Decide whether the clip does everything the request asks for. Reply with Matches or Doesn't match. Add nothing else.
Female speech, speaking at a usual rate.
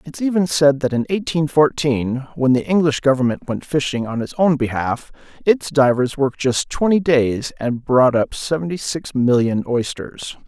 Doesn't match